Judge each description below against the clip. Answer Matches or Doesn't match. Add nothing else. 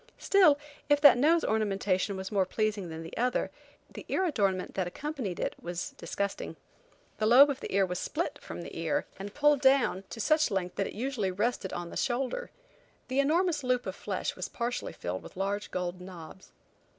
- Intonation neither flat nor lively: Doesn't match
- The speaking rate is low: Doesn't match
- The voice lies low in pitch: Doesn't match